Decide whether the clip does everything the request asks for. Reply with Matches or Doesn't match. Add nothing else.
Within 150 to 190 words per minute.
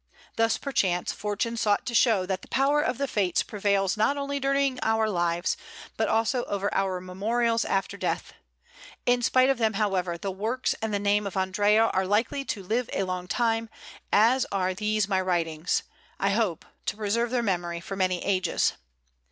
Matches